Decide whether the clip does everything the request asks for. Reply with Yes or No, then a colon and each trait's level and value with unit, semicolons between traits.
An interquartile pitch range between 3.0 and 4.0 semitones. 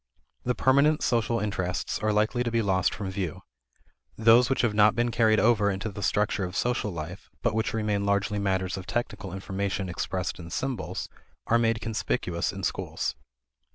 Yes: average, 3.3 semitones